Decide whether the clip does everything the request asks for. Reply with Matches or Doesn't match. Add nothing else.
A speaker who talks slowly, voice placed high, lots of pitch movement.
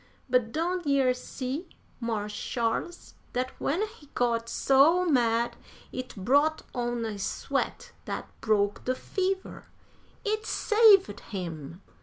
Matches